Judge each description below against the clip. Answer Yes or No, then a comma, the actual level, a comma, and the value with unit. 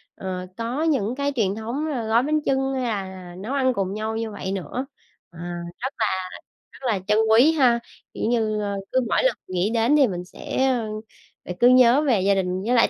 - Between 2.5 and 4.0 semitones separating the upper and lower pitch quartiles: No, average, 4.8 semitones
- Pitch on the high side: Yes, high, 230 Hz